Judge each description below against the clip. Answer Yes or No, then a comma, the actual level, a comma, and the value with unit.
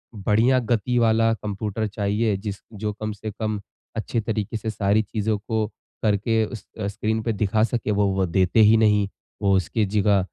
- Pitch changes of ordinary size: No, narrow, 1.6 semitones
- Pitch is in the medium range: No, low, 105 Hz